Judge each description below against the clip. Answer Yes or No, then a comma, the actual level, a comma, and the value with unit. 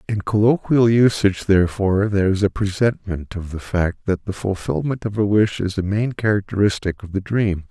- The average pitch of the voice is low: Yes, low, 100 Hz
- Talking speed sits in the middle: Yes, average, 185 wpm